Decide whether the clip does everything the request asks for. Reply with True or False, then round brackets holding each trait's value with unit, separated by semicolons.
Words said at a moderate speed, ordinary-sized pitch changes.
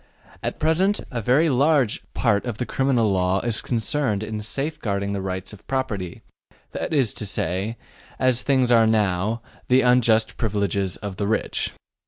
True (160 wpm; 4.3 semitones)